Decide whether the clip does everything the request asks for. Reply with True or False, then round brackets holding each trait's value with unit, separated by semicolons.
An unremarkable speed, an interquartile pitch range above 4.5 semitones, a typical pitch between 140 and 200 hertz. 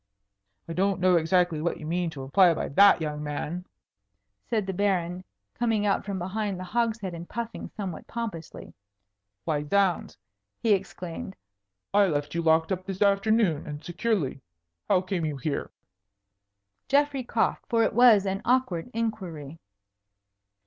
False (150 wpm; 4.2 semitones; 185 Hz)